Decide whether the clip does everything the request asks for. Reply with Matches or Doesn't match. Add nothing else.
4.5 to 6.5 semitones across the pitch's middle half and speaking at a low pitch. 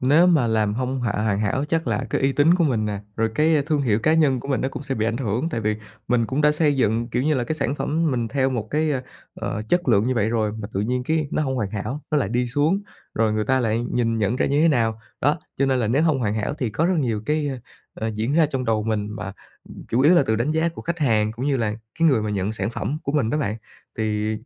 Matches